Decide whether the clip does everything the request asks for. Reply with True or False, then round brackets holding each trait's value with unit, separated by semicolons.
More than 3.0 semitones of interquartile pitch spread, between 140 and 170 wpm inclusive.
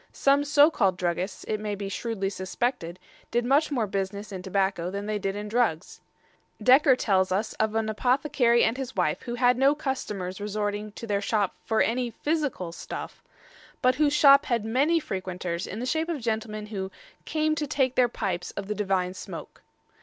False (5.0 semitones; 185 wpm)